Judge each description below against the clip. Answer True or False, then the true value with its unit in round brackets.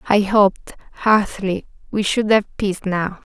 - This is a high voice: True (200 Hz)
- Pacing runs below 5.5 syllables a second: True (4.9 syllables/s)